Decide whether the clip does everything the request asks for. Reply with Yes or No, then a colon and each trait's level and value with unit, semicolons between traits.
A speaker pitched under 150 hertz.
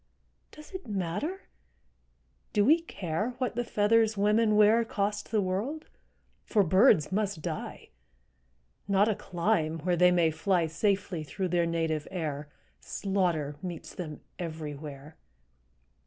No: high, 190 Hz